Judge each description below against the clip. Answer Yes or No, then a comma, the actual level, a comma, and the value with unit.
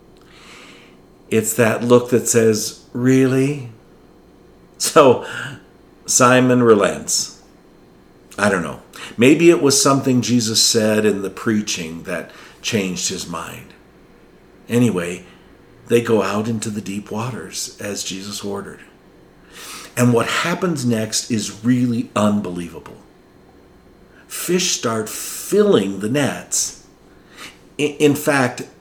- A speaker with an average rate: No, slow, 105 wpm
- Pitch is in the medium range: No, low, 115 Hz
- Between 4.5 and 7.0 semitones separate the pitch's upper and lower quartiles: No, average, 3.4 semitones